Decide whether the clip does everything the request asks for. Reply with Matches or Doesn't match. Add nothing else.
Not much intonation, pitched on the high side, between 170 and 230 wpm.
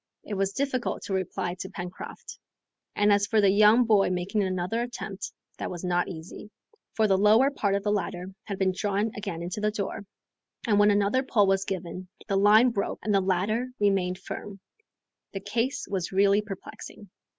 Matches